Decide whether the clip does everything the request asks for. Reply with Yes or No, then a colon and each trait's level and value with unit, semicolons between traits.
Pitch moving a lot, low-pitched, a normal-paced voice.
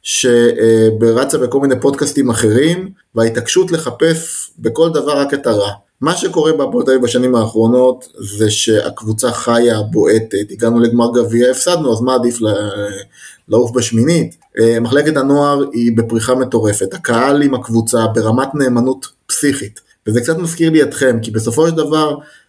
No: average, 3.9 semitones; low, 120 Hz; average, 140 wpm